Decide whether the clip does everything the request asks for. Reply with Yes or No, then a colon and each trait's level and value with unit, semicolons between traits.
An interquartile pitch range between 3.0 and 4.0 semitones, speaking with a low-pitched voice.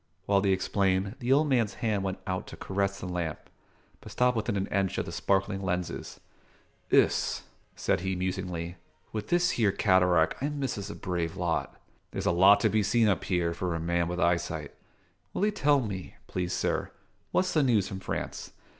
Yes: average, 3.4 semitones; very low, 95 Hz